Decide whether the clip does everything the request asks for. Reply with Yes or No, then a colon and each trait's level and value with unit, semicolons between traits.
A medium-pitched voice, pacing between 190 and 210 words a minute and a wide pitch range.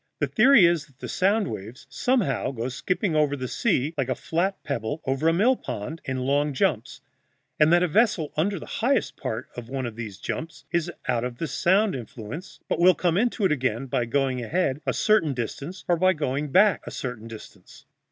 Yes: medium, 150 Hz; average, 200 wpm; wide, 6.2 semitones